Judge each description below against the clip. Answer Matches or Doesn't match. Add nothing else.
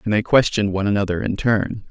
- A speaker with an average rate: Doesn't match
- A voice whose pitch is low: Matches